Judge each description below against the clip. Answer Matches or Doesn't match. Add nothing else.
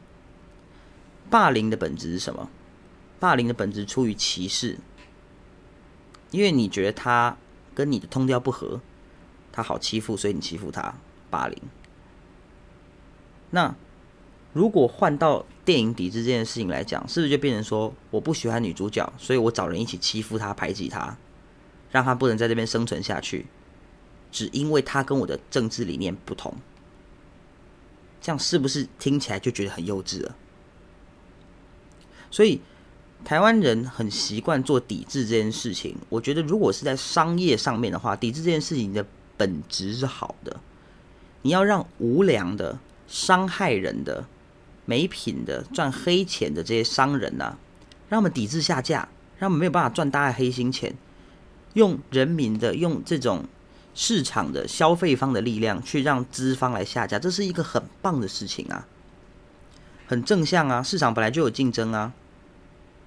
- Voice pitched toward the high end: Doesn't match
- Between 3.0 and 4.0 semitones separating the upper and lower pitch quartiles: Doesn't match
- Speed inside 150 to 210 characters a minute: Doesn't match